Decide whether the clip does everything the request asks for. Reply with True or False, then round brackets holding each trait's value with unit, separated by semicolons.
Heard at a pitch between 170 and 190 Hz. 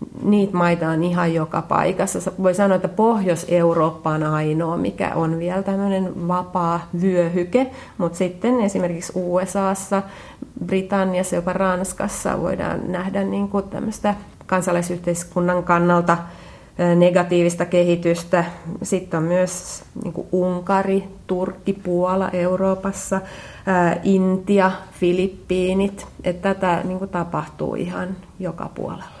True (185 Hz)